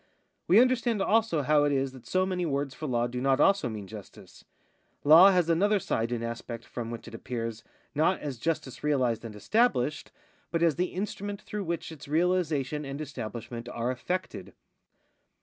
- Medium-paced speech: Yes, average, 175 wpm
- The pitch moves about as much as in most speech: No, wide, 6.9 semitones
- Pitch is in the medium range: Yes, medium, 145 Hz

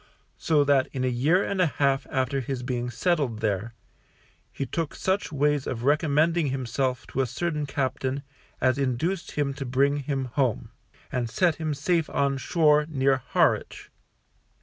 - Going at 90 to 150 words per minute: No, average, 160 wpm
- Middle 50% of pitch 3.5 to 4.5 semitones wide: No, average, 2.7 semitones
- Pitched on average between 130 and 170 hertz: Yes, medium, 140 Hz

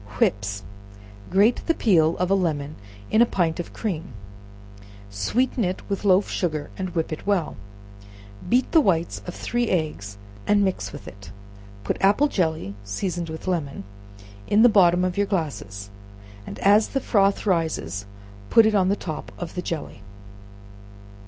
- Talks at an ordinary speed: Yes, average, 160 wpm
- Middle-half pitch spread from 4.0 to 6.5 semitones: Yes, average, 4.6 semitones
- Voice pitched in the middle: Yes, medium, 180 Hz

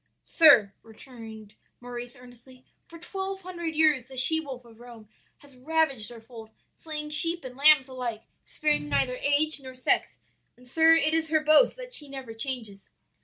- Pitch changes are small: No, average, 4.6 semitones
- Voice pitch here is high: Yes, very high, 265 Hz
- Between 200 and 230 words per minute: No, average, 170 wpm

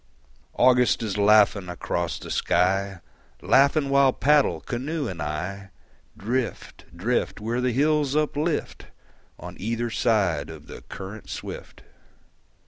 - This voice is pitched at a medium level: No, low, 115 Hz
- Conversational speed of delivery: No, slow, 120 wpm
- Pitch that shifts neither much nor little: No, wide, 5.9 semitones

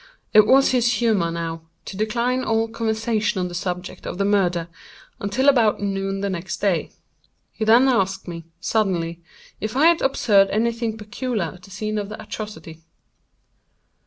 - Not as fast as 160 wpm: No, average, 165 wpm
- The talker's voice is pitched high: Yes, high, 210 Hz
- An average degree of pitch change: Yes, average, 3.6 semitones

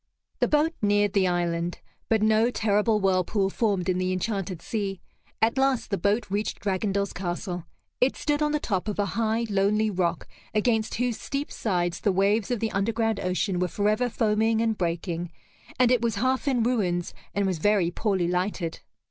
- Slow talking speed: No, average, 180 wpm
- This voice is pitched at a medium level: No, high, 205 Hz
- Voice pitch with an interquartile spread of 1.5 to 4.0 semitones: Yes, average, 3.5 semitones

